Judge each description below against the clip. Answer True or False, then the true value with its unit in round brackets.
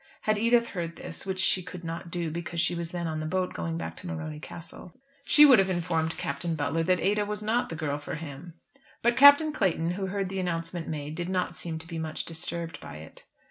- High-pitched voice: False (170 Hz)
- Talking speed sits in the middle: False (230 wpm)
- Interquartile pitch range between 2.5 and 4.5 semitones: True (2.8 semitones)